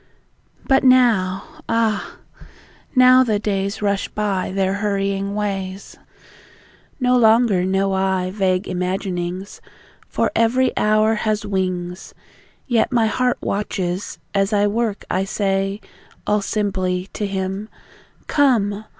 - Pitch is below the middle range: No, high, 200 Hz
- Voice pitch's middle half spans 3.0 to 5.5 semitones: No, narrow, 2.5 semitones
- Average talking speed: No, slow, 115 wpm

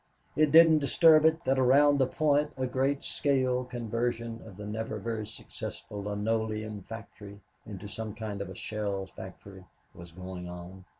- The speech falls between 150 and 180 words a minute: Yes, average, 160 wpm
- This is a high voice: No, low, 110 Hz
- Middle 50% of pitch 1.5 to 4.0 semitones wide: No, average, 4.6 semitones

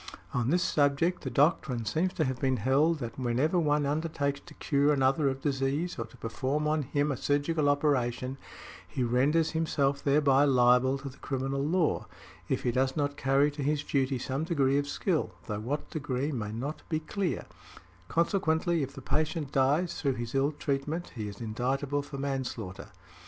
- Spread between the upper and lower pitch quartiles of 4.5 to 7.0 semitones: No, narrow, 2.6 semitones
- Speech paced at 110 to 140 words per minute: No, average, 180 wpm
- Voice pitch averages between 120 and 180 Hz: Yes, medium, 140 Hz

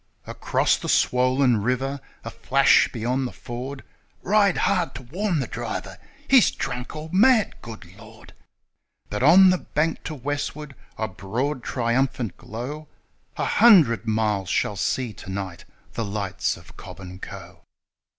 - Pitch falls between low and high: No, low, 125 Hz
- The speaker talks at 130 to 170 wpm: Yes, average, 150 wpm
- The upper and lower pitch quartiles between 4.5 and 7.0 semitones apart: Yes, wide, 5.4 semitones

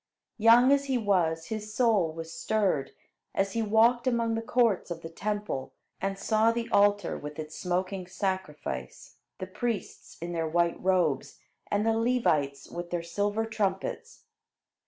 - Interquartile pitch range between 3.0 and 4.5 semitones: No, average, 4.9 semitones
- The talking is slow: No, average, 155 wpm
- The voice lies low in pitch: No, high, 195 Hz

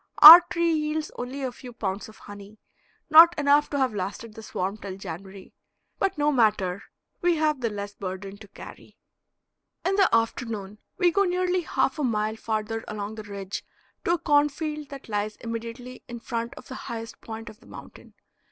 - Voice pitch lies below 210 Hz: No, high, 230 Hz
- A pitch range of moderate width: No, wide, 6.2 semitones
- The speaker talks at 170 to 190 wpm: Yes, average, 180 wpm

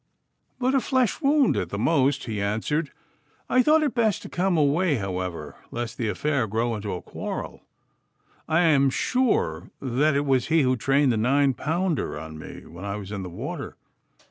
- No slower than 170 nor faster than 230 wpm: Yes, average, 185 wpm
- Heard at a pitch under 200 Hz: Yes, low, 135 Hz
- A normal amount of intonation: No, wide, 8.0 semitones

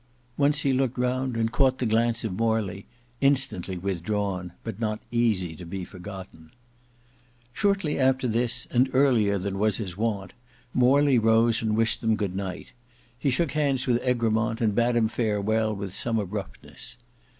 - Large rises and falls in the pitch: No, average, 3.8 semitones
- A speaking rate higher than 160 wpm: No, average, 155 wpm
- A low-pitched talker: Yes, low, 115 Hz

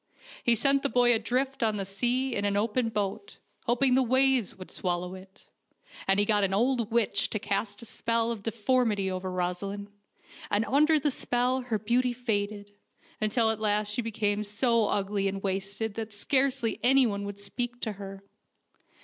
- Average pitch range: Yes, average, 3.3 semitones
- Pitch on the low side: No, high, 220 Hz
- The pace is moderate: Yes, average, 175 wpm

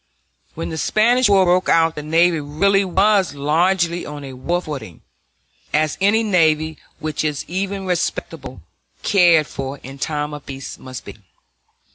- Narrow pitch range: No, average, 4.3 semitones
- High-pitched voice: No, medium, 165 Hz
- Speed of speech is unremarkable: Yes, average, 150 wpm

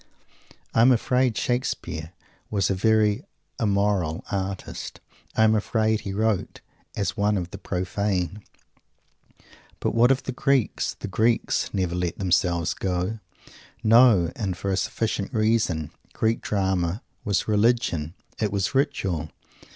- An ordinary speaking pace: No, slow, 130 wpm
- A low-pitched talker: Yes, low, 100 Hz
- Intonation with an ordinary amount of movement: Yes, average, 3.5 semitones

